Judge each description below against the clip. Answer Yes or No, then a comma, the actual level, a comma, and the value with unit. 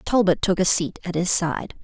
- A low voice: No, medium, 180 Hz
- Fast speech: Yes, fast, 230 wpm